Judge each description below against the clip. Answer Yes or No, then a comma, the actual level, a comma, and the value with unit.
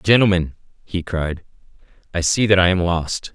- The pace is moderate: Yes, average, 160 wpm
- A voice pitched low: Yes, very low, 90 Hz